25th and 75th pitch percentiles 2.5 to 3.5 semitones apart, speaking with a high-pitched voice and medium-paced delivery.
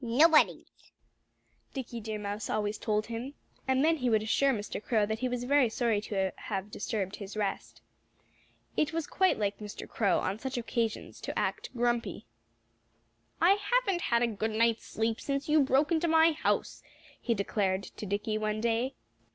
No: average, 4.3 semitones; high, 230 Hz; average, 170 wpm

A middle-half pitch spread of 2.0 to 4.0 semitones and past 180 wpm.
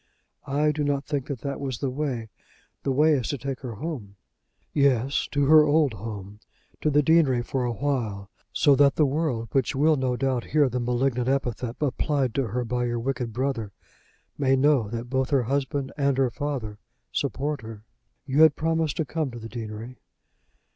Yes: average, 3.2 semitones; average, 190 wpm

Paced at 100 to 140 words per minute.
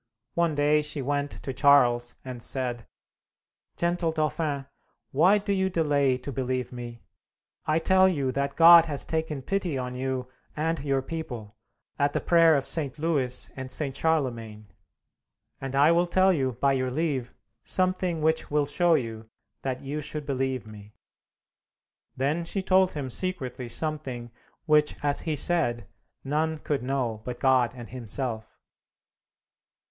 No: average, 150 wpm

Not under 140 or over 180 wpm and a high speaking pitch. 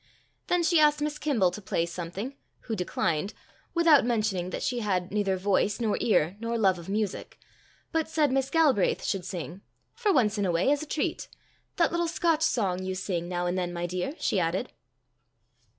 No: average, 190 wpm; high, 210 Hz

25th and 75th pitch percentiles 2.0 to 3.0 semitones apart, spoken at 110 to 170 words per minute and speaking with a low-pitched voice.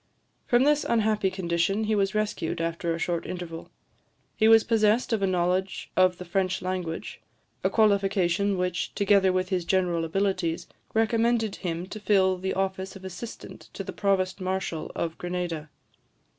No: narrow, 2.6 semitones; average, 155 wpm; high, 190 Hz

